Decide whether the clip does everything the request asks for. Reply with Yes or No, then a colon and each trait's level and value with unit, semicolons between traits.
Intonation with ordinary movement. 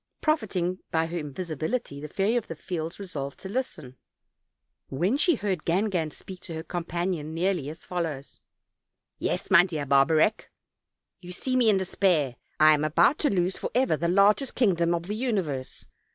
Yes: average, 4.3 semitones